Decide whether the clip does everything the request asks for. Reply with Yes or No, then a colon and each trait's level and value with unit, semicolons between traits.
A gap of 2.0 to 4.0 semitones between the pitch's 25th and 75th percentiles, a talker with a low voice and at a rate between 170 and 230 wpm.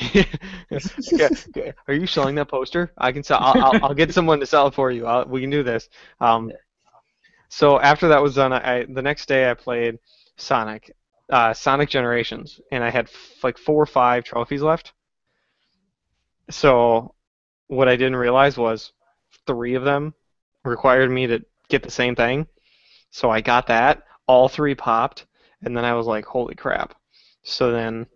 Yes: average, 3.3 semitones; low, 130 Hz; average, 175 wpm